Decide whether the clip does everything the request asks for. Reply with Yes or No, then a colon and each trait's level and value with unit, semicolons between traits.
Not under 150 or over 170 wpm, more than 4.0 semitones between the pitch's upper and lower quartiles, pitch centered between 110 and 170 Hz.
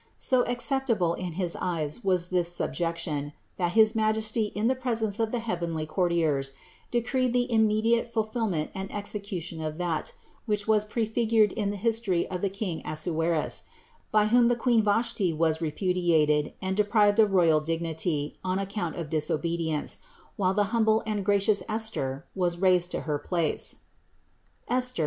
No: average, 155 wpm; average, 4.8 semitones; high, 195 Hz